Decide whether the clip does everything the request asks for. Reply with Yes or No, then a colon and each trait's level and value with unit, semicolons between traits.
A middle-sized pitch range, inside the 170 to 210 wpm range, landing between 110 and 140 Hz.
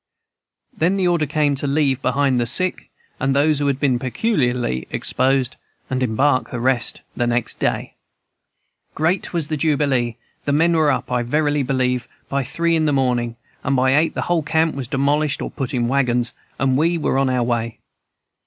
Yes: average, 3.2 semitones; average, 180 wpm; low, 135 Hz